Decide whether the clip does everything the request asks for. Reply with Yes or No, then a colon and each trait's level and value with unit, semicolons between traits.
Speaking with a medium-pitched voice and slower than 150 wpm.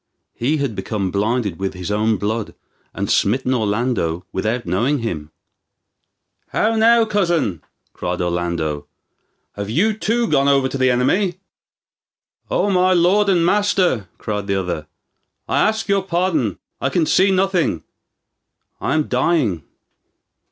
No: low, 125 Hz; slow, 135 wpm